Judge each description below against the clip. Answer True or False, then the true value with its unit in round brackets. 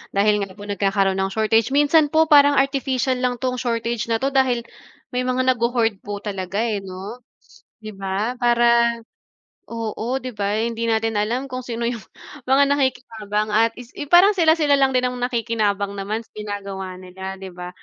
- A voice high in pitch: True (230 Hz)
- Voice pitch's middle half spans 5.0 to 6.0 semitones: False (3.8 semitones)